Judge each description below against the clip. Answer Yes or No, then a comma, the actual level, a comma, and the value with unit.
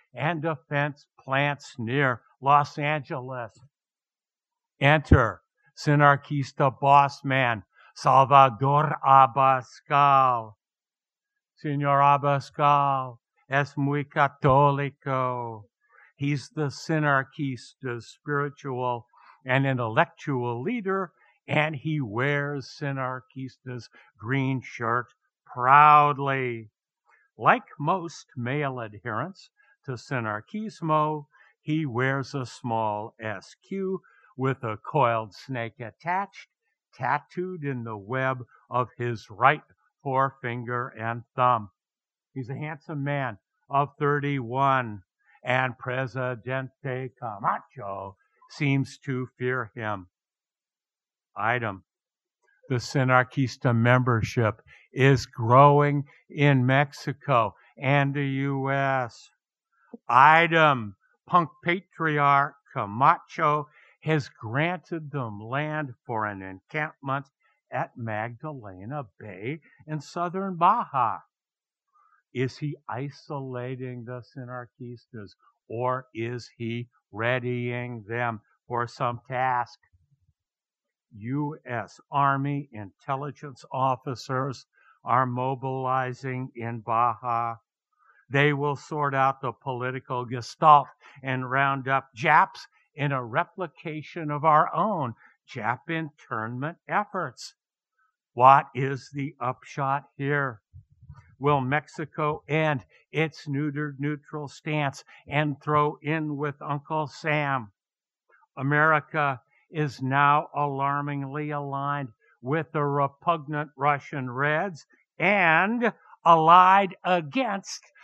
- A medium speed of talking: No, slow, 85 wpm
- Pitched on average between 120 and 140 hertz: Yes, low, 135 Hz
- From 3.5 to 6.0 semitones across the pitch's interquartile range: No, average, 3.1 semitones